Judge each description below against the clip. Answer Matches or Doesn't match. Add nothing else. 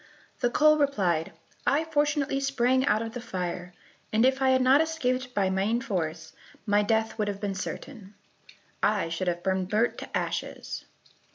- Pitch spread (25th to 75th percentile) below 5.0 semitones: Doesn't match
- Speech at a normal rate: Matches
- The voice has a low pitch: Doesn't match